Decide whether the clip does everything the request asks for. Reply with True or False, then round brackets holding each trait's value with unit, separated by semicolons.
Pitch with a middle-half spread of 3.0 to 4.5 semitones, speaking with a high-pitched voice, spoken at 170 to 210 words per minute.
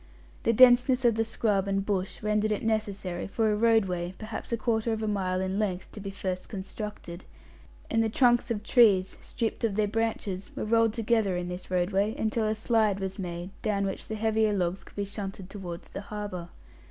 False (2.6 semitones; 210 Hz; 200 wpm)